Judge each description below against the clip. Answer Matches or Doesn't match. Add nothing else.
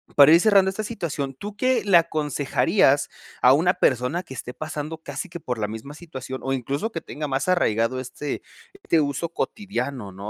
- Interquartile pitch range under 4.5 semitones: Doesn't match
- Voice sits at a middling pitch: Matches